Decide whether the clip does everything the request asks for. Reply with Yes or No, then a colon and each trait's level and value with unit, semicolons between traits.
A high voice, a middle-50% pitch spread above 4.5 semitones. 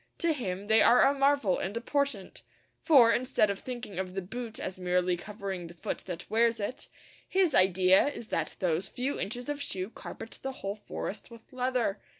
Yes: high, 220 Hz; average, 5.1 semitones